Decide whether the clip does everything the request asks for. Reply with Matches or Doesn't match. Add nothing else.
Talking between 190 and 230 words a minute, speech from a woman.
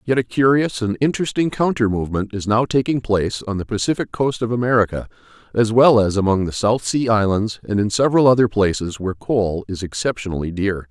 Doesn't match